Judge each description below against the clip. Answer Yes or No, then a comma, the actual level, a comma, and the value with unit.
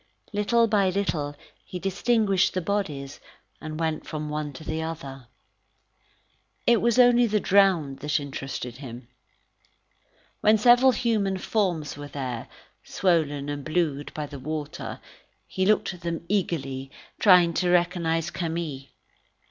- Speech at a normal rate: No, slow, 130 wpm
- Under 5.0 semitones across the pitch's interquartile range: No, average, 5.3 semitones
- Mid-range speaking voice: Yes, medium, 165 Hz